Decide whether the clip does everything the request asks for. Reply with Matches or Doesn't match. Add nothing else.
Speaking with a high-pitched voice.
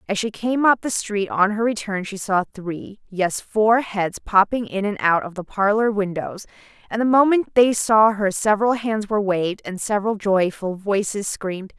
Matches